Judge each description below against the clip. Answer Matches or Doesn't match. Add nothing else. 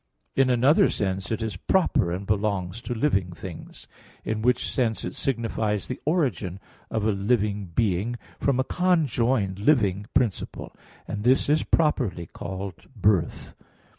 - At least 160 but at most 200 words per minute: Doesn't match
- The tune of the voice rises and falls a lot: Doesn't match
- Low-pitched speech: Matches